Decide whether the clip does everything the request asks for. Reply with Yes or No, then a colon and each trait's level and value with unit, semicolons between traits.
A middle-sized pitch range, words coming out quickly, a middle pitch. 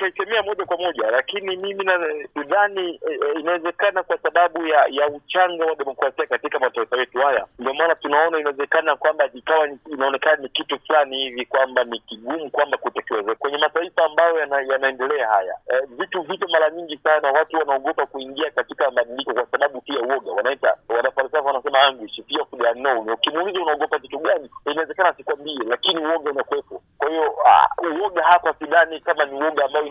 Yes: average, 4.2 semitones; fast, 155 wpm; medium, 155 Hz